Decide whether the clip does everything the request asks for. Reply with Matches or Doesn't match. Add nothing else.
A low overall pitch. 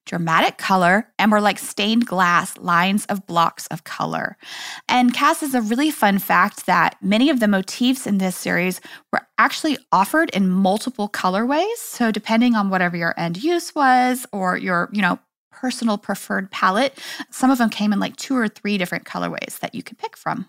Doesn't match